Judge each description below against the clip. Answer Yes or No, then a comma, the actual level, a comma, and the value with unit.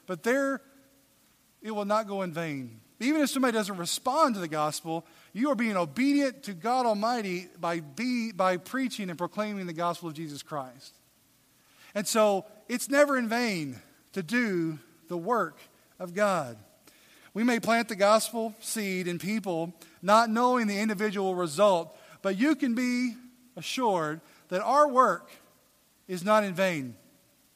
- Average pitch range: No, wide, 5.9 semitones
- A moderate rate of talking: Yes, average, 155 wpm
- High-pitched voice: Yes, high, 205 Hz